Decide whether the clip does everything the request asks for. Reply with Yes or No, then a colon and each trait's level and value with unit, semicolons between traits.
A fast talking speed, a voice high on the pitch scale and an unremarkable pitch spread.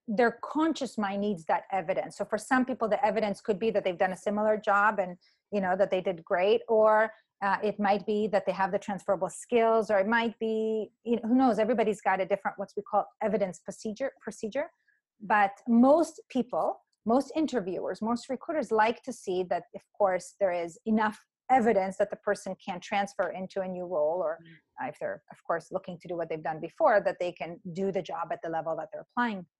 Yes: fast, 215 wpm; high, 205 Hz; average, 3.0 semitones